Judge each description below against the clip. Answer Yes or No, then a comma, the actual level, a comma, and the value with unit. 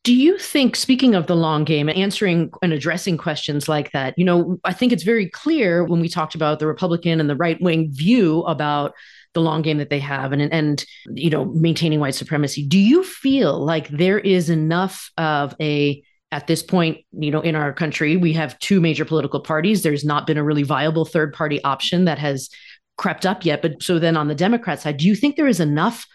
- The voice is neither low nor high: Yes, medium, 160 Hz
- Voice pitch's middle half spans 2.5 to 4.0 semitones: Yes, average, 3.4 semitones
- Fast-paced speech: Yes, fast, 225 wpm